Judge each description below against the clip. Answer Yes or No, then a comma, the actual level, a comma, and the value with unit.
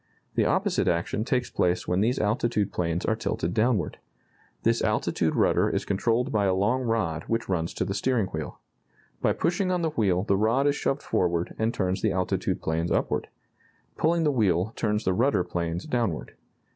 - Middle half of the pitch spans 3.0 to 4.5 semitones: No, average, 5.1 semitones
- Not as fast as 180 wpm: No, average, 185 wpm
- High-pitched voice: No, low, 105 Hz